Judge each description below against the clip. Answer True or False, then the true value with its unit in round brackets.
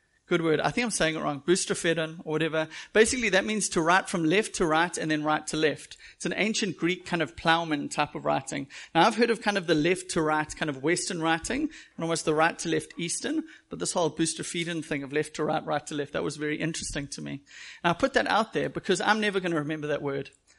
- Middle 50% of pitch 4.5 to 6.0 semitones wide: False (3.6 semitones)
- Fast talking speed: True (255 wpm)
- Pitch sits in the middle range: True (165 Hz)